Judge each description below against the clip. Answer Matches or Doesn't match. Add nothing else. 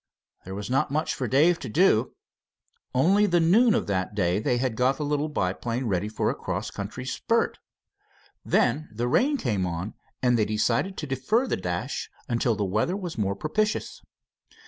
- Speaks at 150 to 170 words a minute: Doesn't match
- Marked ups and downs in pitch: Matches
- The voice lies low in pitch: Matches